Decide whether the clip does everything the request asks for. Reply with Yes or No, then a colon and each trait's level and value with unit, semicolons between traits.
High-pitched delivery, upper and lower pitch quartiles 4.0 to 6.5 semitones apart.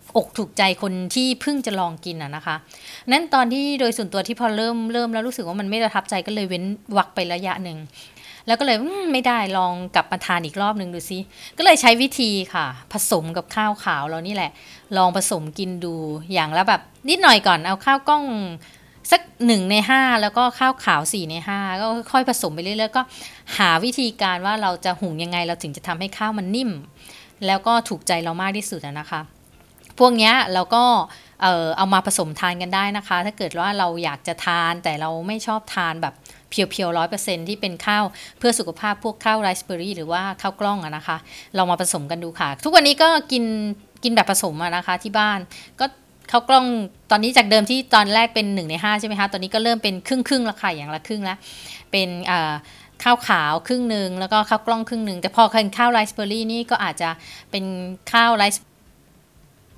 Yes: high, 200 Hz; average, 4.3 semitones